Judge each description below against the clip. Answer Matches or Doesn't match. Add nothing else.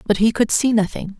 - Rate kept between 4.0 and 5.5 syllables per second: Doesn't match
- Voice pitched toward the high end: Matches